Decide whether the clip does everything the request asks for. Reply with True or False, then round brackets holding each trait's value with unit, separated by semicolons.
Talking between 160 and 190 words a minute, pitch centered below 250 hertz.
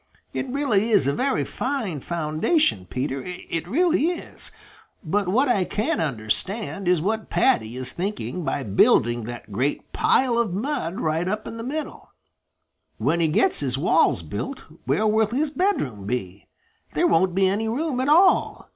True (165 wpm; 190 Hz)